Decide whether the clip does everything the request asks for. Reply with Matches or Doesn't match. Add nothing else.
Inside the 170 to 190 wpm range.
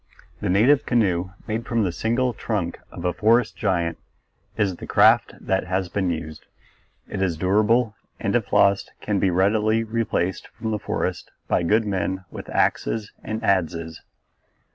Doesn't match